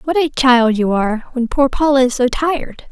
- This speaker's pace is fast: Yes, fast, 225 wpm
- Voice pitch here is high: Yes, very high, 260 Hz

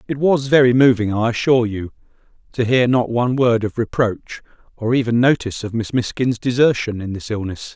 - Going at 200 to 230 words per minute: No, average, 180 wpm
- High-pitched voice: No, low, 120 Hz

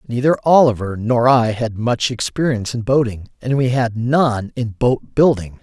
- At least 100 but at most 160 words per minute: No, average, 170 wpm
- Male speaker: Yes, male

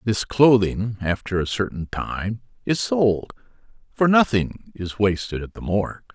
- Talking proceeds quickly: No, slow, 135 wpm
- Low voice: Yes, low, 105 Hz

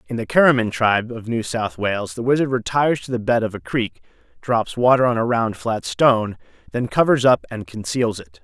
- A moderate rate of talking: No, fast, 215 wpm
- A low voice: Yes, low, 115 Hz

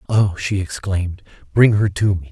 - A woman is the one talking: No, male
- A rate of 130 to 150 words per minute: No, average, 180 wpm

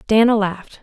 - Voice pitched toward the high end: Yes, high, 210 Hz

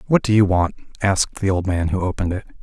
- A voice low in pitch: Yes, very low, 95 Hz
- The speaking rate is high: Yes, fast, 250 wpm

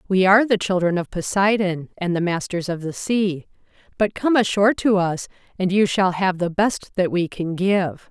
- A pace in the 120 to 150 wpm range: No, average, 200 wpm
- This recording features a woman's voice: Yes, female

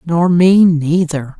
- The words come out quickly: No, slow, 130 wpm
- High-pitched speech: No, medium, 165 Hz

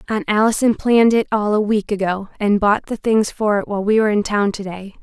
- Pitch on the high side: Yes, high, 210 Hz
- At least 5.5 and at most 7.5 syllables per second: Yes, 5.9 syllables/s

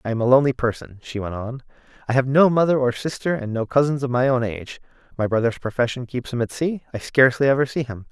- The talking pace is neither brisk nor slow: No, fast, 245 wpm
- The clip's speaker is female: No, male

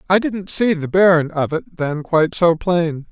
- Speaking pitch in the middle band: Yes, medium, 170 Hz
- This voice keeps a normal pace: No, fast, 210 wpm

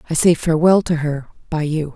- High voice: No, medium, 160 Hz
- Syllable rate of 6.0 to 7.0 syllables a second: No, 5.8 syllables/s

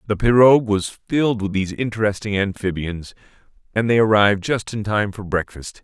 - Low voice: Yes, low, 105 Hz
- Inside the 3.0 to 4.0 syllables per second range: No, 5.6 syllables/s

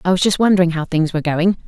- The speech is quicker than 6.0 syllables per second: Yes, 7.3 syllables/s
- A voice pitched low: No, medium, 175 Hz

